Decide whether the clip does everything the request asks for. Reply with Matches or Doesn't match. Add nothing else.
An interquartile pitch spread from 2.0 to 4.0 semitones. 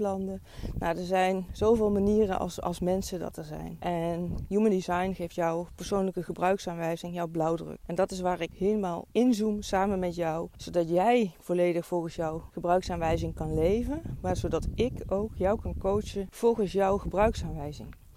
Matches